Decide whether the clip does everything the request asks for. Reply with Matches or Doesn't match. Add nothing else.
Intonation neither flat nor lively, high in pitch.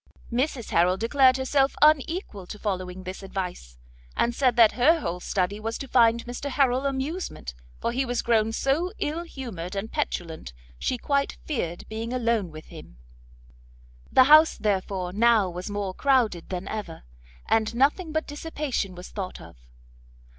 Doesn't match